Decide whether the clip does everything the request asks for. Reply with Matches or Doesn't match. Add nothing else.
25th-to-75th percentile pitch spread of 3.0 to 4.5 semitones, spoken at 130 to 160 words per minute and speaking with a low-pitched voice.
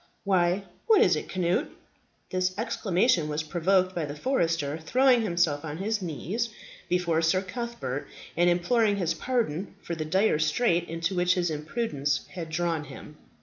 Doesn't match